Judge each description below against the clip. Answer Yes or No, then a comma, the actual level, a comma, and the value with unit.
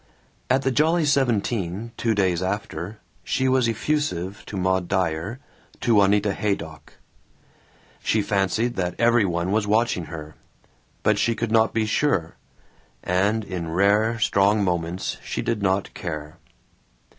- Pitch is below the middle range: Yes, low, 100 Hz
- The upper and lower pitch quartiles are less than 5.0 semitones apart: Yes, average, 4.1 semitones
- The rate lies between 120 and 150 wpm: Yes, slow, 135 wpm